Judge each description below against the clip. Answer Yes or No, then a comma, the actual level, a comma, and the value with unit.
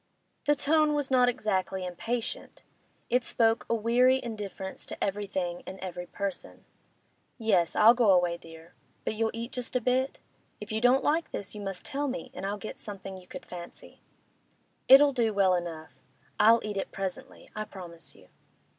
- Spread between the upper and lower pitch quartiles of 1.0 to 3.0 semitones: No, average, 4.6 semitones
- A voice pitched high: Yes, high, 210 Hz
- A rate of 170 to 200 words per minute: Yes, average, 175 wpm